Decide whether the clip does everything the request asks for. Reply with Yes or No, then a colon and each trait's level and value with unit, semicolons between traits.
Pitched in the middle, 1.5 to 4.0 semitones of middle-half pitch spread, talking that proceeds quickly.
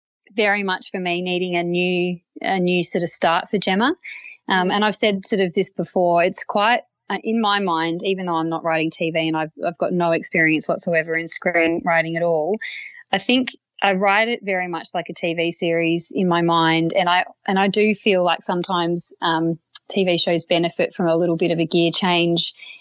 Yes: medium, 175 Hz; average, 2.7 semitones; fast, 210 wpm